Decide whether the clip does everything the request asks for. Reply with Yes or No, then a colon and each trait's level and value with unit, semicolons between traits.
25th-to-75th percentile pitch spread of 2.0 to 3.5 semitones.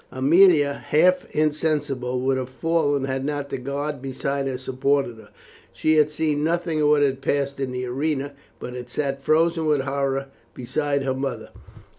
Yes: narrow, 2.4 semitones